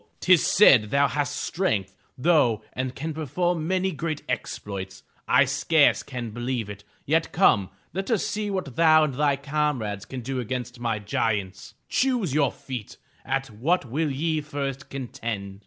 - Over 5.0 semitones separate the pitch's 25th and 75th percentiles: Yes, wide, 5.5 semitones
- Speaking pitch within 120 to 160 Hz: Yes, low, 135 Hz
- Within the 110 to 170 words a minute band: Yes, average, 160 wpm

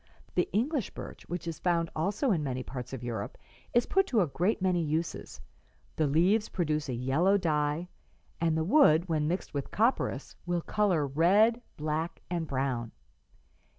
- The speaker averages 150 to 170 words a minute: Yes, average, 165 wpm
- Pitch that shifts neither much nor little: Yes, average, 4.5 semitones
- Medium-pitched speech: Yes, medium, 165 Hz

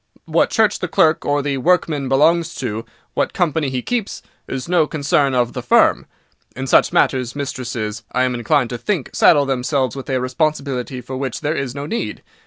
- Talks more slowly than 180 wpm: No, average, 190 wpm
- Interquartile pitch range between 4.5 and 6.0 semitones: No, average, 3.4 semitones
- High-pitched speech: No, low, 135 Hz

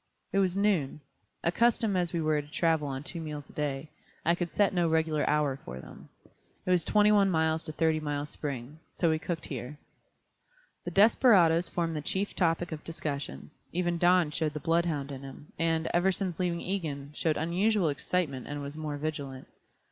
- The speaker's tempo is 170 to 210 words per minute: Yes, average, 185 wpm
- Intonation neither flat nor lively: Yes, average, 3.1 semitones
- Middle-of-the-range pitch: Yes, medium, 160 Hz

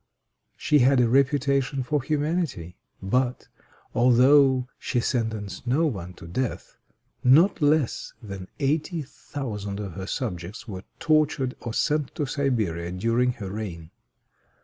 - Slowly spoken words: Yes, slow, 125 wpm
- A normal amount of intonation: No, wide, 5.7 semitones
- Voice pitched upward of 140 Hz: No, low, 125 Hz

